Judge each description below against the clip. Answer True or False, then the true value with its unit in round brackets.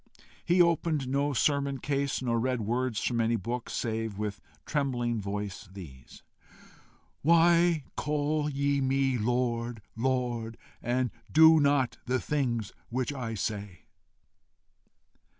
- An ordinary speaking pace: False (115 wpm)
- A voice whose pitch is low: True (125 Hz)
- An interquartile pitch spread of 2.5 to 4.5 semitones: True (3.9 semitones)